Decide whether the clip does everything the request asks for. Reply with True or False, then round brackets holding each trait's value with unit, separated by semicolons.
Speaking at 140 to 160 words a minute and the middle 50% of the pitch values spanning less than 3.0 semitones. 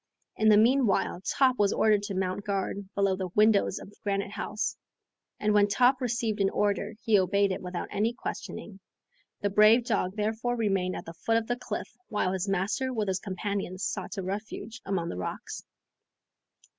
False (180 wpm; 2.4 semitones)